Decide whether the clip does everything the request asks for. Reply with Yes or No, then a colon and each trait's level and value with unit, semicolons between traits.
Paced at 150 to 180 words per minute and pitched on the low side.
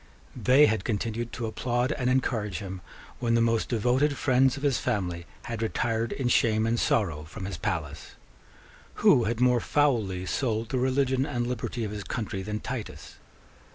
Yes: average, 170 wpm; low, 115 Hz